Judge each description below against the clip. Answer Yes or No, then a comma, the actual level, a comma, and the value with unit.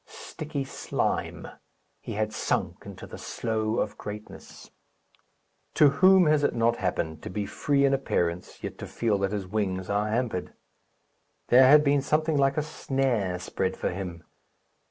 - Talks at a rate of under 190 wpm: Yes, average, 155 wpm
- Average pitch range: No, wide, 6.2 semitones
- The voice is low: Yes, low, 115 Hz